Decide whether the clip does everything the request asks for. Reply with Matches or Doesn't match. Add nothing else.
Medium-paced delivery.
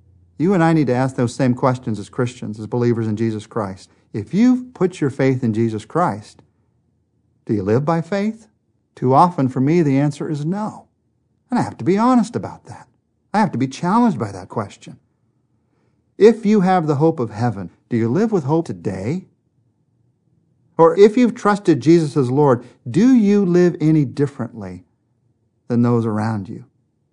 Matches